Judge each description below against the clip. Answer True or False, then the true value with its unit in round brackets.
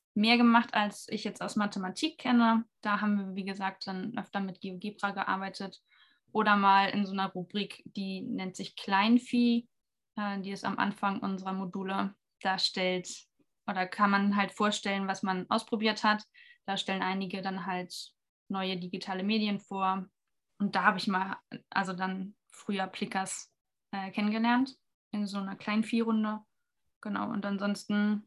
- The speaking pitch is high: True (200 Hz)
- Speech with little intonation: True (1.8 semitones)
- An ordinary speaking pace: True (150 wpm)